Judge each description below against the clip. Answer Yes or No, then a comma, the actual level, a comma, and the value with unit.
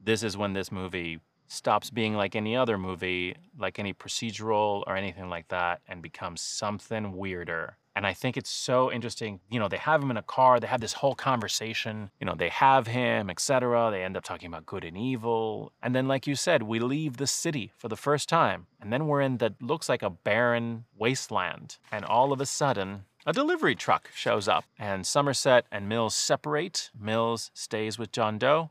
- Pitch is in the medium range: No, low, 115 Hz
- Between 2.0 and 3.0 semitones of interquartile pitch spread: No, average, 4.2 semitones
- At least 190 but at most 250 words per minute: Yes, fast, 205 wpm